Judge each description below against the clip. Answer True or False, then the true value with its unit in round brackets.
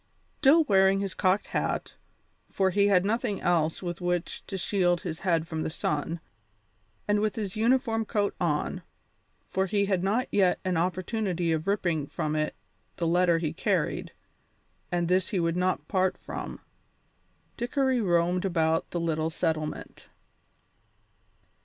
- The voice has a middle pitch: True (180 Hz)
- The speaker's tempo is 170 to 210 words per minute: False (145 wpm)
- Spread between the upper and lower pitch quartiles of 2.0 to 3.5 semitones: True (3.2 semitones)